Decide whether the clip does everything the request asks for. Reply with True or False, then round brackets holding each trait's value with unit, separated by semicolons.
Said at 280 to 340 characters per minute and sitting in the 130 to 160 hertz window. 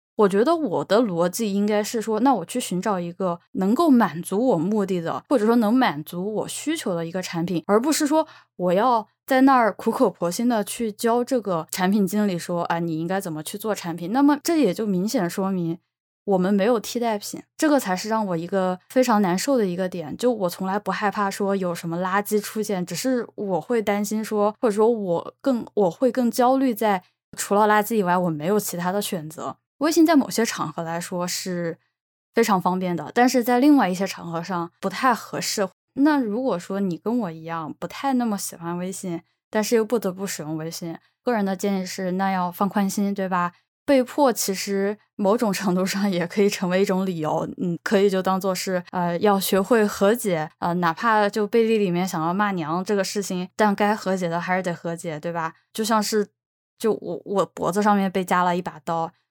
False (300 characters per minute; 200 Hz)